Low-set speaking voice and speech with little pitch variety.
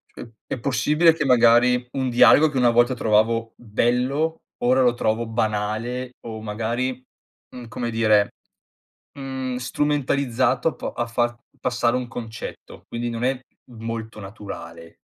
Yes: low, 120 Hz; narrow, 2.2 semitones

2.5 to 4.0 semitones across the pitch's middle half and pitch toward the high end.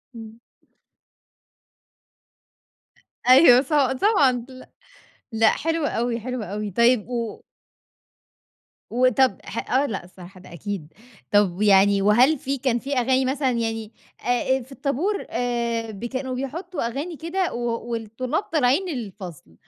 Yes: average, 3.6 semitones; high, 245 Hz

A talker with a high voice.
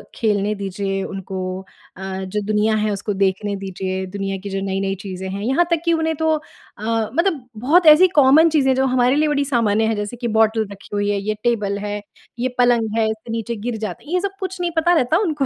Yes: high, 220 Hz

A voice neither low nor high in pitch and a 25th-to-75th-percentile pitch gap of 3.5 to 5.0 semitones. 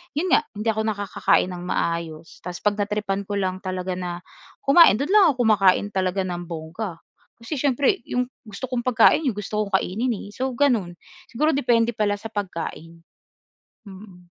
No: high, 205 Hz; average, 4.6 semitones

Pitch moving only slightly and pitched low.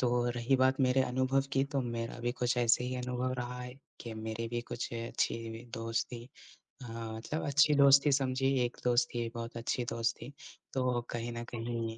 Yes: narrow, 1.9 semitones; low, 120 Hz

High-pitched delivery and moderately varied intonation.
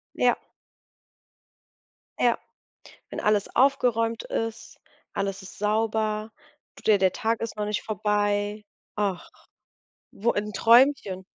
No: high, 210 Hz; narrow, 1.7 semitones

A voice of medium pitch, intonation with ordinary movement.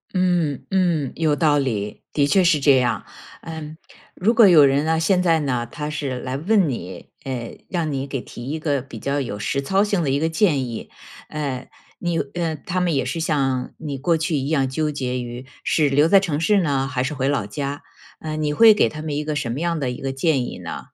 Yes: medium, 145 Hz; average, 3.6 semitones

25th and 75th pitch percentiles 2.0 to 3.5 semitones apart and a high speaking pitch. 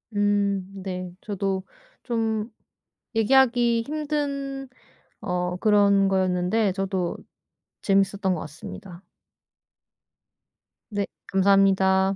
Yes: average, 2.9 semitones; high, 195 Hz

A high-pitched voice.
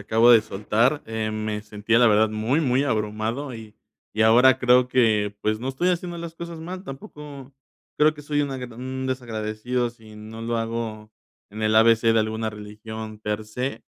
No: low, 115 Hz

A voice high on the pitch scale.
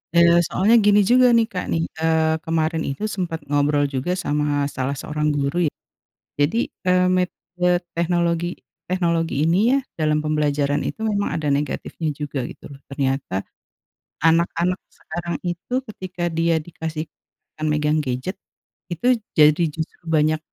No: medium, 160 Hz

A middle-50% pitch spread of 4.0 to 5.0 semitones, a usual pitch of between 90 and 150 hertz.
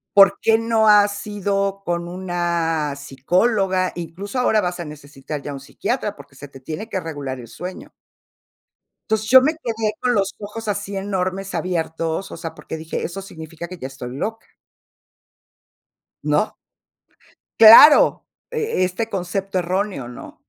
No: average, 4.3 semitones; medium, 185 Hz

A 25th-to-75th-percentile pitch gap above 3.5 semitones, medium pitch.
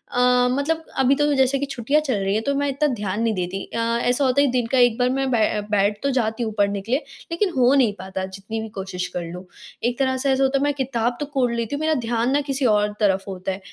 No: average, 4.6 semitones; high, 245 Hz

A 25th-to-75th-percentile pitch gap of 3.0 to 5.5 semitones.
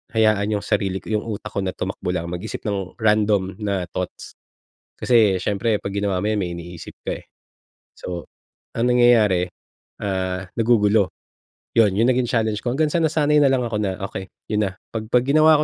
Yes: average, 3.7 semitones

